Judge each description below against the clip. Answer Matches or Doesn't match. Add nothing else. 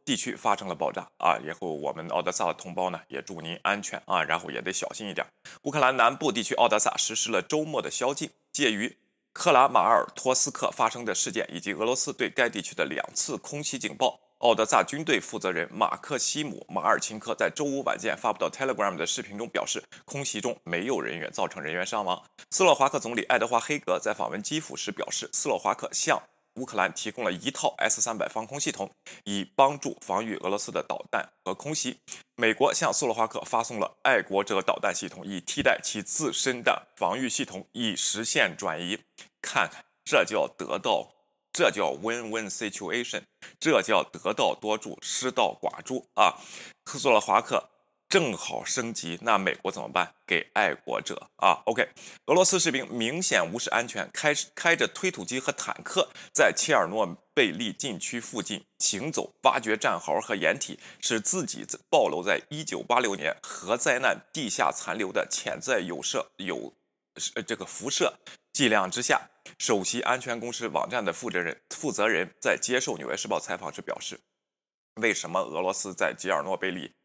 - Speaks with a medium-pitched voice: Doesn't match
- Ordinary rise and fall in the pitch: Matches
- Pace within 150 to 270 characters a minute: Doesn't match